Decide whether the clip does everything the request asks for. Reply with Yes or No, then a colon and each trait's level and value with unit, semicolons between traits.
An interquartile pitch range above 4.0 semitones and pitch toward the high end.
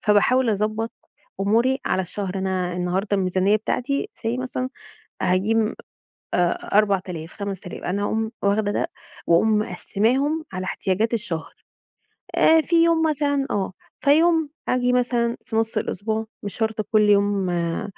Yes: average, 4.4 semitones; high, 215 Hz